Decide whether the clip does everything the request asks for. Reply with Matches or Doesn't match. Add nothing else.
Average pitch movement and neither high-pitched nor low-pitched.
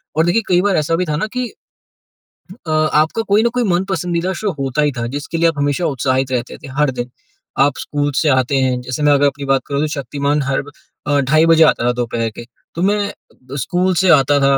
Matches